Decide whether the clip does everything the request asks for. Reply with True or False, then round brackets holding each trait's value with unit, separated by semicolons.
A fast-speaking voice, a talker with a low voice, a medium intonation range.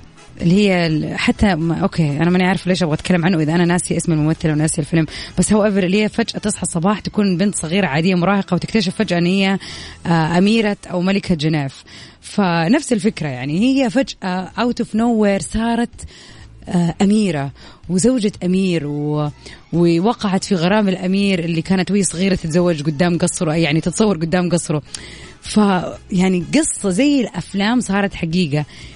False (155 wpm; 185 Hz; 3.5 semitones)